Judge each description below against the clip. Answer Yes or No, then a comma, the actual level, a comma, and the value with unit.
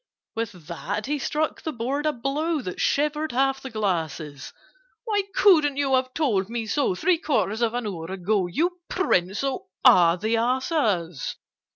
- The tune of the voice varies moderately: No, wide, 7.4 semitones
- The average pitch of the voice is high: Yes, high, 240 Hz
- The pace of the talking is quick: No, average, 165 wpm